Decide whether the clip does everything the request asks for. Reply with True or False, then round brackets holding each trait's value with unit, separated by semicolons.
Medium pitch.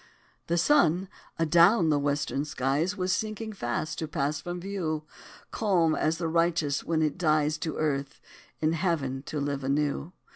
True (155 Hz)